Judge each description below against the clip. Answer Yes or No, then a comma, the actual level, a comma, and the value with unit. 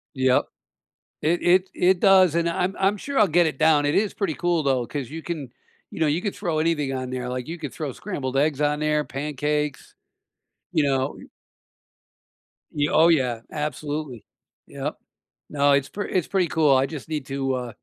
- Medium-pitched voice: Yes, medium, 150 Hz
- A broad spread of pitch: No, average, 3.9 semitones